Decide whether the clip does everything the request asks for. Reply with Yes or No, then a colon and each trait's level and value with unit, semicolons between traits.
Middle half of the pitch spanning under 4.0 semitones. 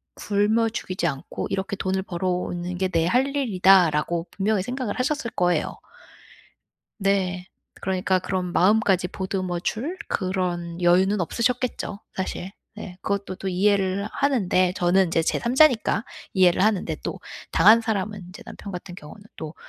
Yes: average, 3.0 semitones